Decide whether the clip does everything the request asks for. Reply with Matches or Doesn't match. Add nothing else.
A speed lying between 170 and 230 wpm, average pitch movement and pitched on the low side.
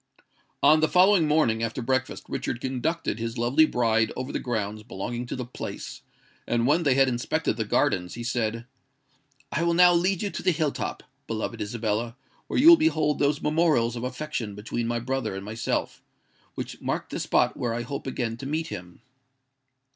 Matches